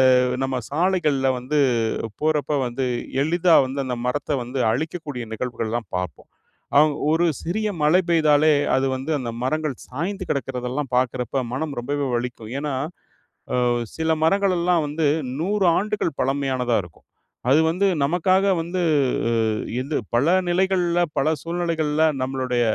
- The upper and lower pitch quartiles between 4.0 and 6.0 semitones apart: Yes, average, 4.7 semitones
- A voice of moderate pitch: Yes, medium, 150 Hz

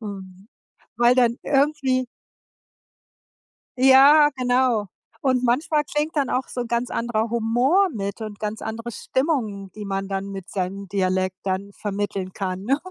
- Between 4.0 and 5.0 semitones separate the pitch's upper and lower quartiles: Yes, average, 4.7 semitones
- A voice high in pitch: Yes, high, 230 Hz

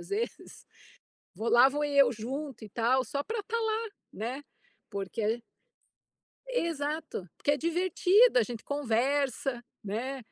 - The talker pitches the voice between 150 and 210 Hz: No, very high, 275 Hz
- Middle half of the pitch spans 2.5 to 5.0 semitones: No, wide, 5.5 semitones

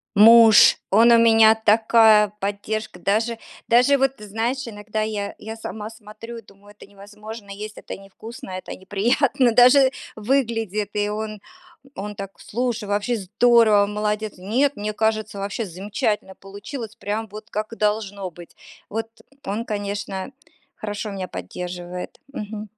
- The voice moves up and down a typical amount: No, narrow, 1.9 semitones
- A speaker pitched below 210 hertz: No, high, 215 Hz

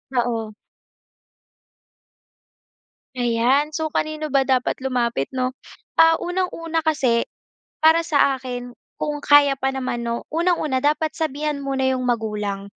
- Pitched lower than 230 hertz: No, very high, 270 Hz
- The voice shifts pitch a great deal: No, average, 4.0 semitones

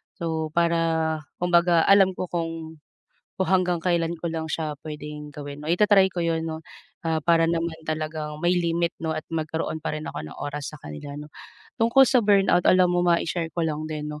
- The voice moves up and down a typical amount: No, narrow, 2.0 semitones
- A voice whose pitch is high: No, medium, 165 Hz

